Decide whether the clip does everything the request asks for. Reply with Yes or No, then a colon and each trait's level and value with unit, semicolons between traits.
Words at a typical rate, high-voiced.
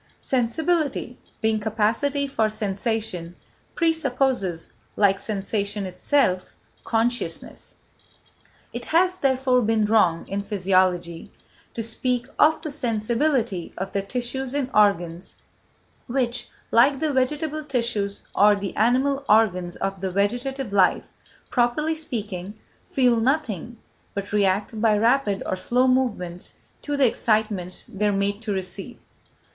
No: slow, 120 wpm; high, 225 Hz